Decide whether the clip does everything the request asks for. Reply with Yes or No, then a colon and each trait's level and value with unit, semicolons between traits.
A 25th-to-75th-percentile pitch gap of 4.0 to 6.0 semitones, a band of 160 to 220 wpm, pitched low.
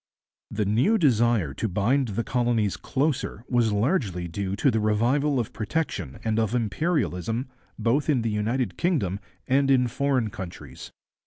No: average, 4.6 semitones; average, 150 wpm; low, 115 Hz